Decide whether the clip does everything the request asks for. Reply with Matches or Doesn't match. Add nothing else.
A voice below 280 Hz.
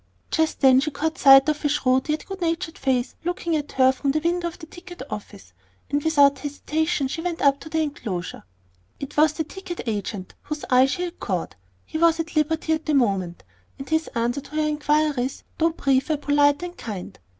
Doesn't match